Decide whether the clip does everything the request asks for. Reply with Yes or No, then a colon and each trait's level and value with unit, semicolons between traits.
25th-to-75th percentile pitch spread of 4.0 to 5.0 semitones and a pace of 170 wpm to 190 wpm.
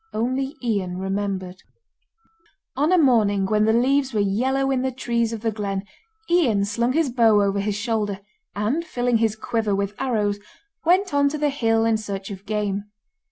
Yes: average, 4.4 semitones; average, 175 wpm